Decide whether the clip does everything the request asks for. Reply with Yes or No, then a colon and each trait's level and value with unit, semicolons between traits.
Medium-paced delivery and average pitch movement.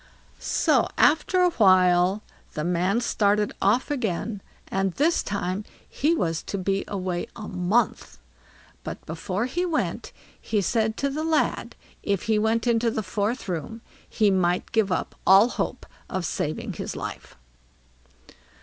Yes: average, 145 wpm; average, 4.1 semitones